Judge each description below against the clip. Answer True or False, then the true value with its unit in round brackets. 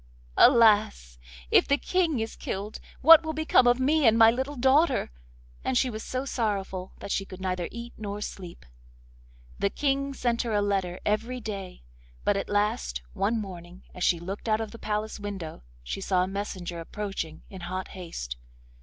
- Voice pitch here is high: True (210 Hz)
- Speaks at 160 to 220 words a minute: True (180 wpm)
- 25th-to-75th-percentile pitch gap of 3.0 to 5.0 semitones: True (4.6 semitones)